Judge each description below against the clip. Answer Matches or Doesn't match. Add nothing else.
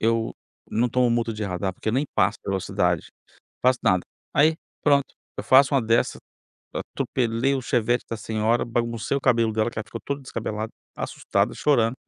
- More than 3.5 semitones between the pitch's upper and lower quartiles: Doesn't match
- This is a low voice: Matches